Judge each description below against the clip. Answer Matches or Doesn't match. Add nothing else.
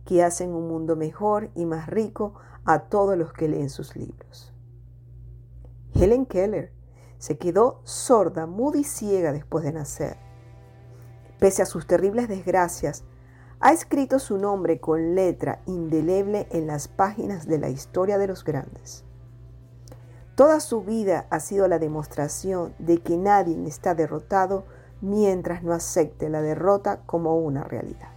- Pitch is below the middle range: Doesn't match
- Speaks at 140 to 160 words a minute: Matches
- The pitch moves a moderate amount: Doesn't match